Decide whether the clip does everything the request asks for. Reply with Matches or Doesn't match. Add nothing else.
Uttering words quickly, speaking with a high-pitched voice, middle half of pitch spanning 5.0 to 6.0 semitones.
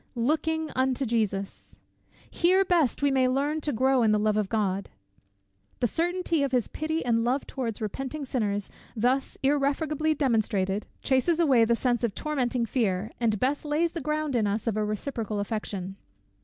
Doesn't match